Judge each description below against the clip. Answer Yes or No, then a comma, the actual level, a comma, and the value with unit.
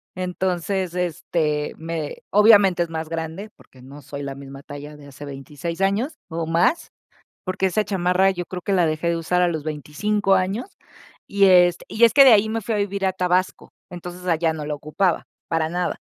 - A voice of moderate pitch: Yes, medium, 175 Hz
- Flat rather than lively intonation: No, average, 3.6 semitones